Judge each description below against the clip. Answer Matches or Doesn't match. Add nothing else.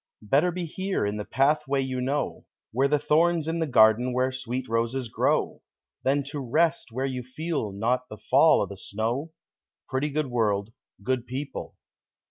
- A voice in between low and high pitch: Doesn't match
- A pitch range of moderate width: Matches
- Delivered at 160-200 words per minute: Matches